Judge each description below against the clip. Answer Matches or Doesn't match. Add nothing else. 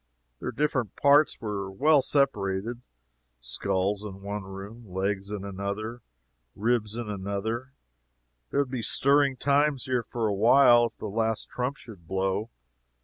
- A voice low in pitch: Matches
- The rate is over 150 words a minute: Doesn't match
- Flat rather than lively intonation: Doesn't match